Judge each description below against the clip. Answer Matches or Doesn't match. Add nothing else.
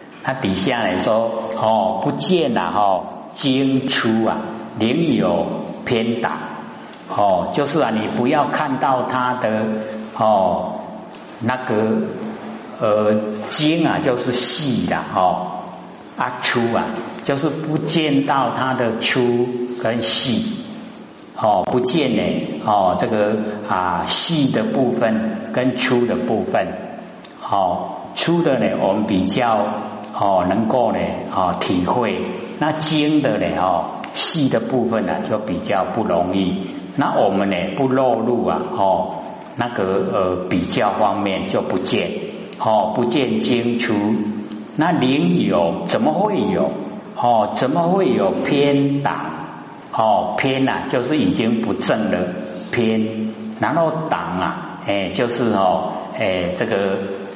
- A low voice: Matches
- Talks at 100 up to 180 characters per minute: Matches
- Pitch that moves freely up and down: Doesn't match